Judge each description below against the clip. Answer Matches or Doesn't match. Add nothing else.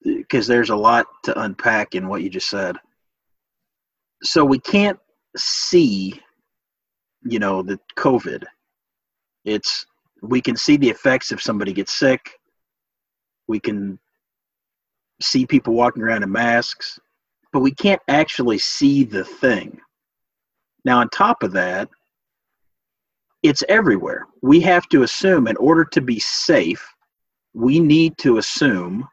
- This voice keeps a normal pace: Doesn't match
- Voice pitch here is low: Doesn't match